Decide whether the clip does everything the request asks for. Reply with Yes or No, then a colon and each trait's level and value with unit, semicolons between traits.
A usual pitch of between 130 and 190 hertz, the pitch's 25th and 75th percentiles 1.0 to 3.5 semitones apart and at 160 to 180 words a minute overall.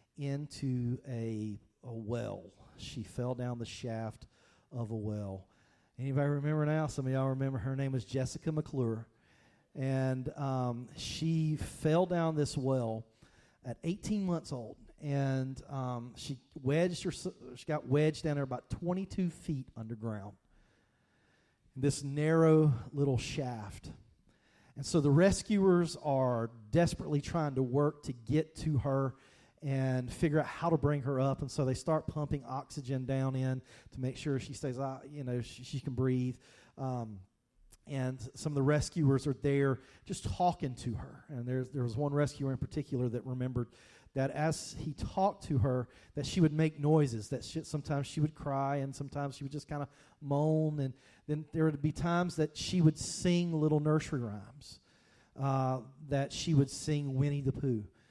Yes: low, 135 Hz; average, 3.2 semitones; average, 170 wpm